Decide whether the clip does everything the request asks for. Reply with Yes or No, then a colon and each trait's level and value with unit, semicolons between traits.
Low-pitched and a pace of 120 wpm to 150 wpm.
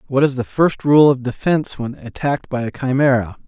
No: low, 130 Hz; fast, 205 wpm